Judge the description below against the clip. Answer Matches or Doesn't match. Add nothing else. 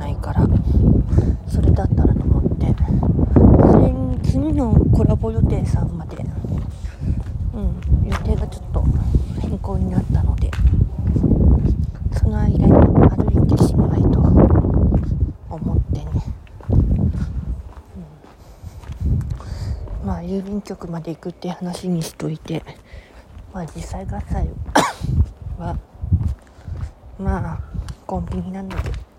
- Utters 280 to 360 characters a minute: Doesn't match